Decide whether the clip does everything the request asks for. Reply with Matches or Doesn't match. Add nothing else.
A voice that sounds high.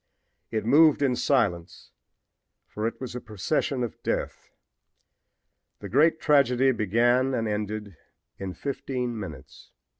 Doesn't match